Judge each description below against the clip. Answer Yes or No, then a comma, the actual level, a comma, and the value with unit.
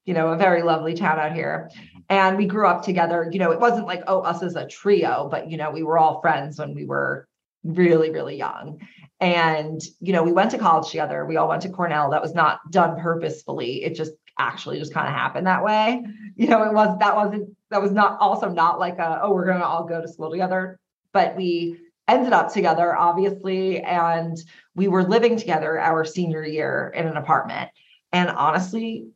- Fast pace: Yes, fast, 210 wpm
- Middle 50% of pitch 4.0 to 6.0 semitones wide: No, average, 3.4 semitones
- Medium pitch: Yes, medium, 175 Hz